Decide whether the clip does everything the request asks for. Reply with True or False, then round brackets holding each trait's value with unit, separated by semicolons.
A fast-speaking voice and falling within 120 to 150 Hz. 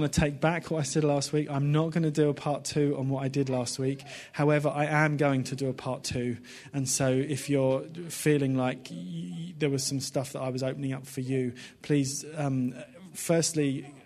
True (220 wpm; 140 Hz)